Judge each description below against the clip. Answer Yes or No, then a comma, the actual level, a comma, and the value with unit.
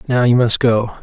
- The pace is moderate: No, fast, 235 wpm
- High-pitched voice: No, low, 120 Hz